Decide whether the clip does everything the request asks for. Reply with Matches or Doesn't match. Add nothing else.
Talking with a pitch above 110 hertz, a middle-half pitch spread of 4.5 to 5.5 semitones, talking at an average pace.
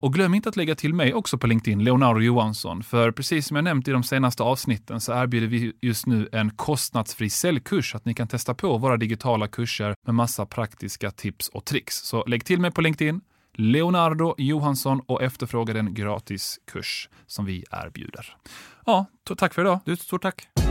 Doesn't match